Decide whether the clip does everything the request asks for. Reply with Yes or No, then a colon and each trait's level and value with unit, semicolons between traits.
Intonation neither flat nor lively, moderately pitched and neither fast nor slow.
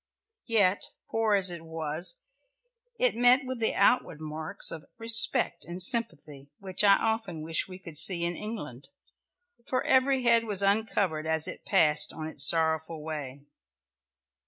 No: wide, 6.0 semitones; medium, 180 Hz; average, 150 wpm